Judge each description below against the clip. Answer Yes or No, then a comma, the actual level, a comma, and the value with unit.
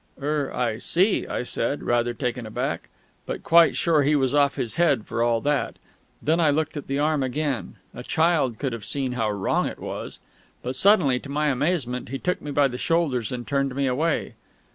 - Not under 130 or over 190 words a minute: No, fast, 205 wpm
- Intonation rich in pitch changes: No, average, 3.6 semitones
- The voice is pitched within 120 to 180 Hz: Yes, medium, 140 Hz